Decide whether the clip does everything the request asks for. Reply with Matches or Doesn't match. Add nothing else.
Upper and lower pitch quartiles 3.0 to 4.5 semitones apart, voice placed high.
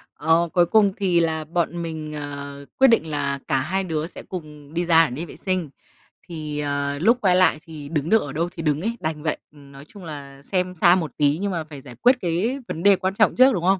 Doesn't match